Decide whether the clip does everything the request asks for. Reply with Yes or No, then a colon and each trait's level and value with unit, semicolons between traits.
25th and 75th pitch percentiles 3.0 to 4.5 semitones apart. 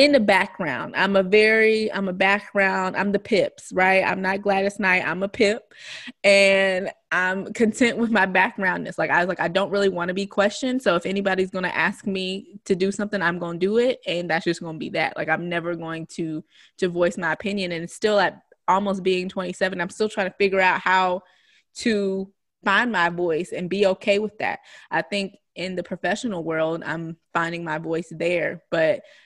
No: narrow, 2.5 semitones